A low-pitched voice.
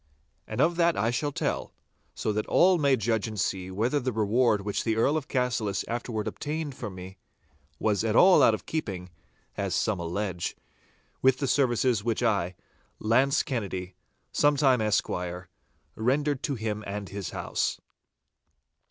Yes: low, 115 Hz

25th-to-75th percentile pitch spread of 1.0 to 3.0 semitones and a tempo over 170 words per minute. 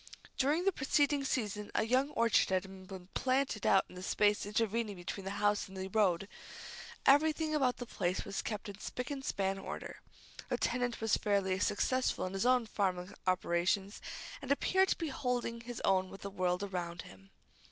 No: average, 5.0 semitones; average, 180 wpm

